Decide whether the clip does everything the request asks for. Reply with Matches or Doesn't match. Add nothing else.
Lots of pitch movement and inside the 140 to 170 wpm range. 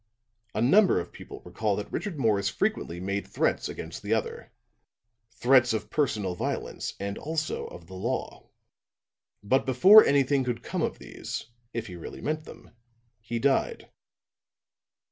Matches